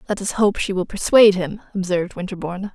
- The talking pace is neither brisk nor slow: Yes, average, 195 wpm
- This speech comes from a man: No, female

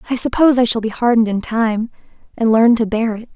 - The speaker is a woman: Yes, female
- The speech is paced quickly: Yes, fast, 235 wpm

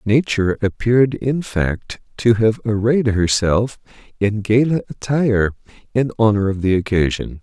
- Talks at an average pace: No, slow, 130 wpm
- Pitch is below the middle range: Yes, low, 110 Hz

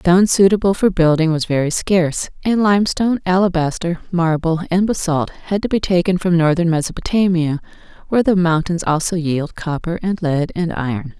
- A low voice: No, medium, 175 Hz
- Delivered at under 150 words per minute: No, average, 160 wpm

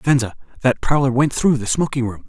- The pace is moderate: No, fast, 210 wpm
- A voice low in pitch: Yes, low, 130 Hz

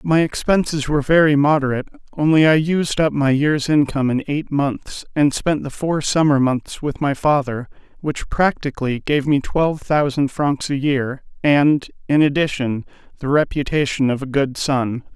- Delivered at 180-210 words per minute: No, average, 165 wpm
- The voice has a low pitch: No, medium, 145 Hz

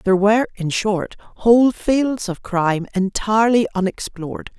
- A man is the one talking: No, female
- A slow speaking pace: Yes, slow, 130 wpm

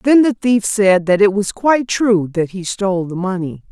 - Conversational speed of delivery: No, fast, 225 wpm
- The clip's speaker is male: No, female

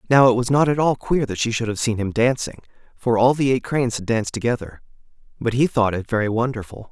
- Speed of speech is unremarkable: No, fast, 245 wpm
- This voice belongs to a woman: No, male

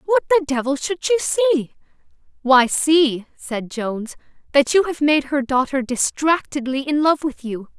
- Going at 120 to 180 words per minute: Yes, average, 160 wpm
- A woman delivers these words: Yes, female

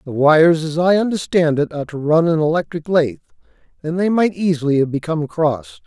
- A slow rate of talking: No, average, 195 wpm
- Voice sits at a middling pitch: Yes, medium, 160 Hz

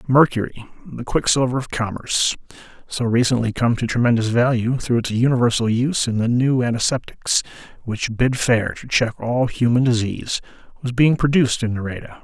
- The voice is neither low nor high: No, low, 120 Hz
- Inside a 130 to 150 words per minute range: Yes, average, 140 wpm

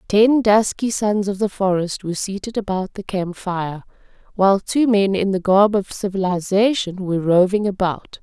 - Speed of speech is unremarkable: Yes, average, 170 wpm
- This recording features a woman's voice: Yes, female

